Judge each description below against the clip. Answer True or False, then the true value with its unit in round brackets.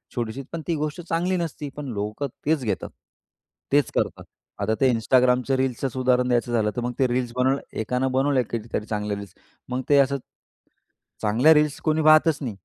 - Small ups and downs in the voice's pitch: False (3.7 semitones)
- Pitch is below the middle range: True (130 Hz)